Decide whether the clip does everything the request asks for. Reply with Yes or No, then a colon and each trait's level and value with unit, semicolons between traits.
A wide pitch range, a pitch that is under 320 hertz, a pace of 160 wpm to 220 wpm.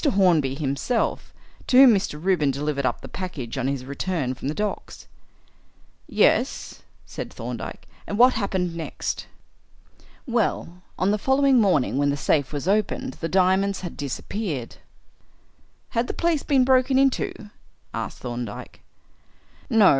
No: wide, 8.2 semitones; medium, 185 Hz; average, 140 wpm